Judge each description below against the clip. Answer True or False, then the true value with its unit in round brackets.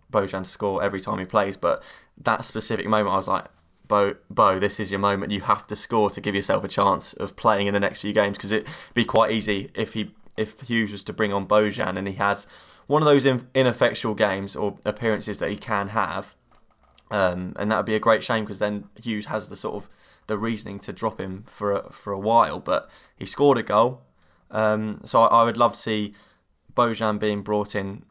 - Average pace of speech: False (225 wpm)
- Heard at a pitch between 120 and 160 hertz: False (105 Hz)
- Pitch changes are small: True (1.9 semitones)